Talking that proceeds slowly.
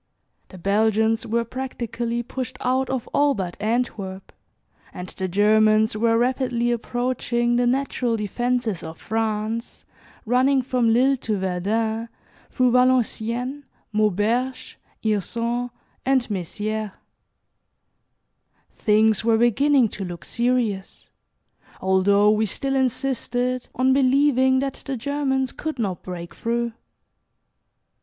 Yes: slow, 110 wpm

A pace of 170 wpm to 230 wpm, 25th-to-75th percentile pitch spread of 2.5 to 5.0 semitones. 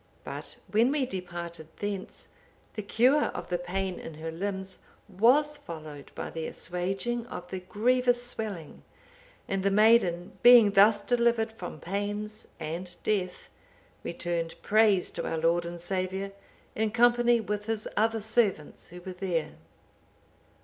No: average, 140 wpm; average, 4.1 semitones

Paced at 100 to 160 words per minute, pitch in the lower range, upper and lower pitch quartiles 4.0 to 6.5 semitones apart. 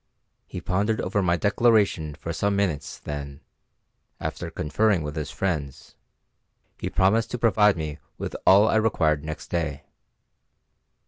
Yes: slow, 135 wpm; very low, 90 Hz; average, 5.3 semitones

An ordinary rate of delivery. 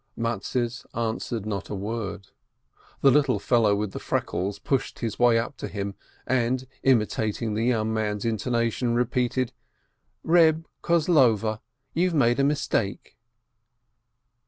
No: slow, 125 wpm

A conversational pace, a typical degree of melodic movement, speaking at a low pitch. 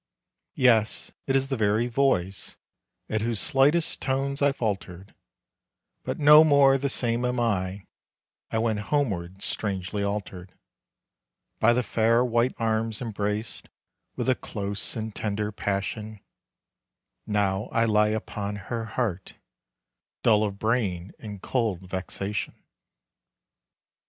No: slow, 120 wpm; average, 3.4 semitones; low, 110 Hz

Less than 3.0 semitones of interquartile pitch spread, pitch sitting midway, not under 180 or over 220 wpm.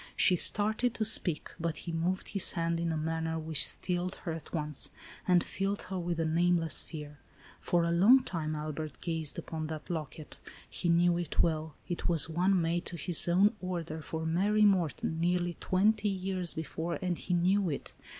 Yes: narrow, 2.4 semitones; medium, 170 Hz; average, 185 wpm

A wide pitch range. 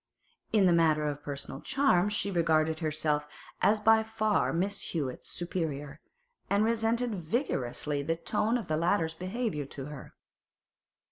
Yes: wide, 5.9 semitones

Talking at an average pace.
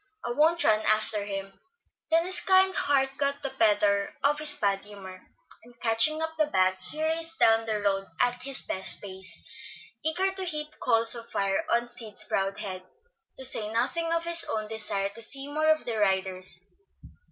Yes: average, 185 wpm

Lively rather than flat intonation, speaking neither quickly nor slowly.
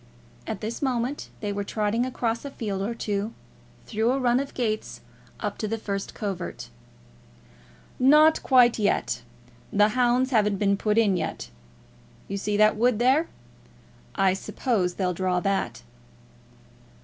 No: average, 3.6 semitones; average, 145 wpm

